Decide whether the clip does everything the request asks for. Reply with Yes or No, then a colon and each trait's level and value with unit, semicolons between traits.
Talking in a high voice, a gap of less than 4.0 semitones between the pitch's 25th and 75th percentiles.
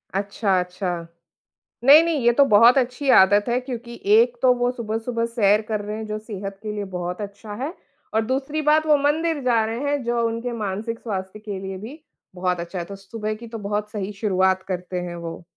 Yes: high, 215 Hz; average, 3.6 semitones